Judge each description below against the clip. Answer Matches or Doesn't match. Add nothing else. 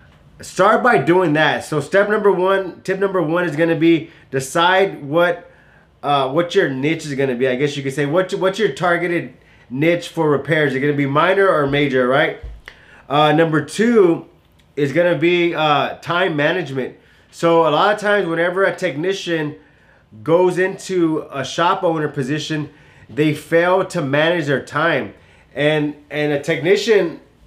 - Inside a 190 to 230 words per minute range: Doesn't match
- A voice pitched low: Doesn't match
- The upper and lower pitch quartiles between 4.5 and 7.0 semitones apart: Doesn't match